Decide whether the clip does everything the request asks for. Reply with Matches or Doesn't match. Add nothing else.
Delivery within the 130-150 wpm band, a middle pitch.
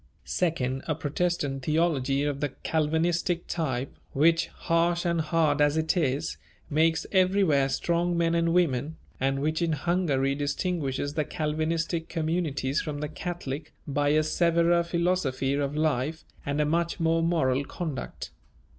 Matches